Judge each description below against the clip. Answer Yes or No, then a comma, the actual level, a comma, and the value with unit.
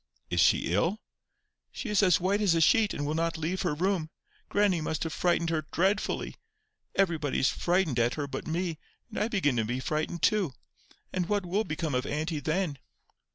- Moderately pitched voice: Yes, medium, 165 Hz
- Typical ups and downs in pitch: Yes, average, 3.9 semitones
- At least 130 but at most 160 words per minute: No, average, 195 wpm